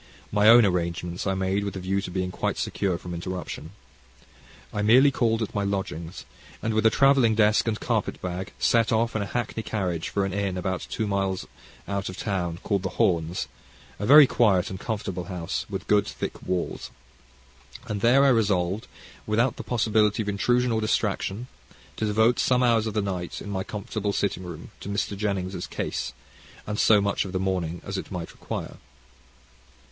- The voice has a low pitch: Yes, low, 100 Hz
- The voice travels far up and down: No, average, 3.0 semitones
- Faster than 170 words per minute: Yes, average, 185 wpm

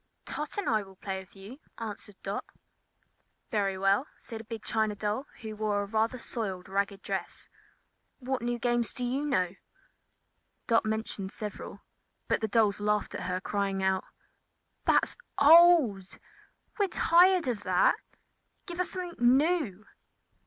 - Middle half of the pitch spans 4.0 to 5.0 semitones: Yes, average, 4.7 semitones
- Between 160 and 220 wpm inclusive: No, average, 150 wpm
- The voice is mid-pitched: No, high, 220 Hz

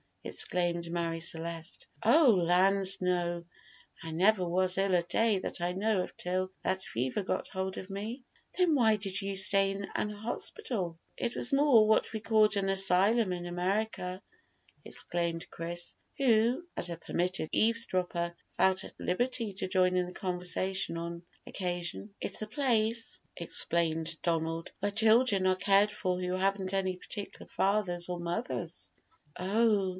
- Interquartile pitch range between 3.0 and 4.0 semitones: Yes, average, 3.3 semitones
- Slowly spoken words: No, average, 150 wpm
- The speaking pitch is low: No, high, 190 Hz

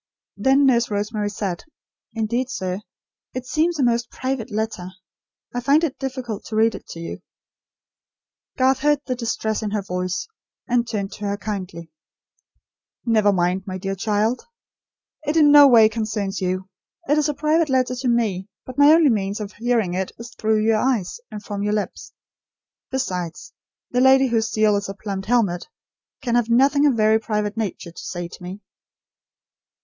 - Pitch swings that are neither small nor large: Yes, average, 4.2 semitones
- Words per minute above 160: Yes, average, 175 wpm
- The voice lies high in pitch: Yes, high, 220 Hz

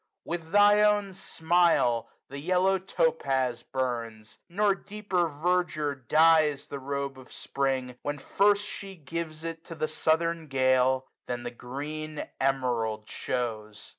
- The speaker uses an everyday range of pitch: Yes, average, 4.9 semitones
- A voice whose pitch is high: No, medium, 150 Hz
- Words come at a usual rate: No, slow, 130 wpm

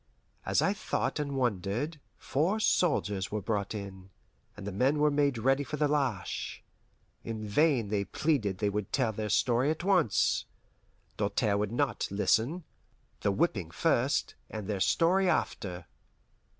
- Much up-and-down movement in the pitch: Yes, wide, 6.5 semitones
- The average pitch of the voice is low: Yes, low, 115 Hz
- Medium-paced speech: Yes, average, 150 wpm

